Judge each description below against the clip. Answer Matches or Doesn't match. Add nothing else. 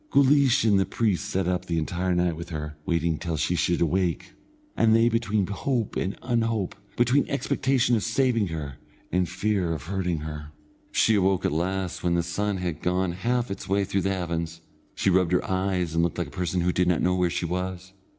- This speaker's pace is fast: Matches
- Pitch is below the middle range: Matches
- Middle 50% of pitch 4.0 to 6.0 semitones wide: Doesn't match